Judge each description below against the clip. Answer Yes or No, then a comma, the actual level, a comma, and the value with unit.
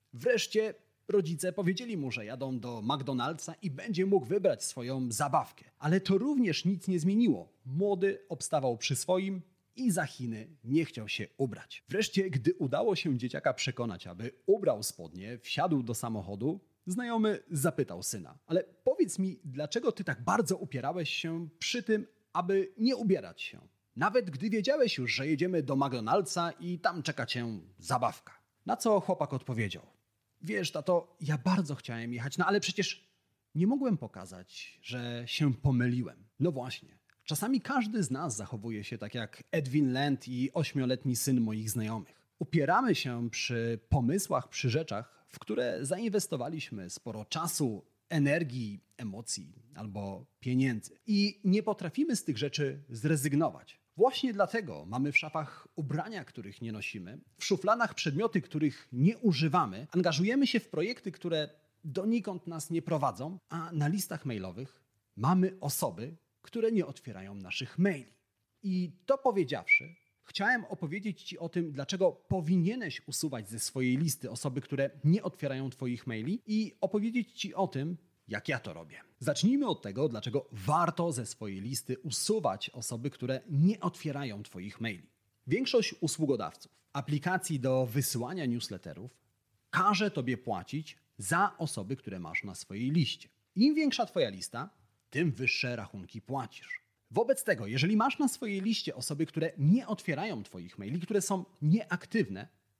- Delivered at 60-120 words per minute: No, average, 145 wpm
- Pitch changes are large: Yes, wide, 7.5 semitones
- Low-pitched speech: No, medium, 150 Hz